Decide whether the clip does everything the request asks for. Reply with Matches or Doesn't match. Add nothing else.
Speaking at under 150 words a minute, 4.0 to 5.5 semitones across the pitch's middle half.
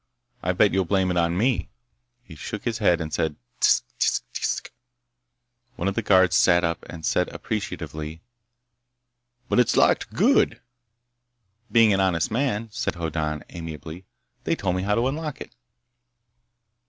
Doesn't match